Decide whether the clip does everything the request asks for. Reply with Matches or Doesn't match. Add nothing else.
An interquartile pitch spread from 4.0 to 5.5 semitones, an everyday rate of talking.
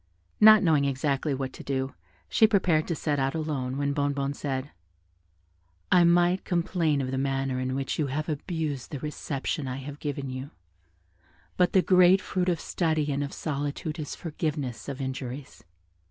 Doesn't match